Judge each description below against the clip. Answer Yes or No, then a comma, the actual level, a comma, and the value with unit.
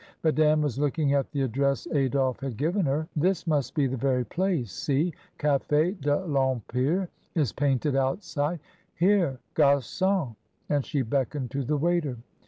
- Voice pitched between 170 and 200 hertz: No, medium, 145 Hz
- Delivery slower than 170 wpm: Yes, average, 155 wpm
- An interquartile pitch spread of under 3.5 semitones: Yes, average, 3.0 semitones